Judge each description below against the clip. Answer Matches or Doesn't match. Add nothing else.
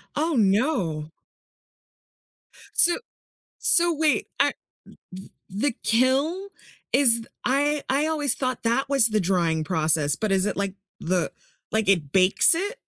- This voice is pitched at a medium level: Doesn't match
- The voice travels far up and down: Matches